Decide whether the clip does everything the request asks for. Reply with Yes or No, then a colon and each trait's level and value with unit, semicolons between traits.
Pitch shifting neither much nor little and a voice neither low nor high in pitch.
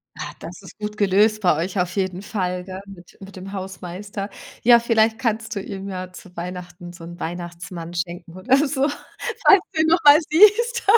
No: average, 4.1 semitones; high, 195 Hz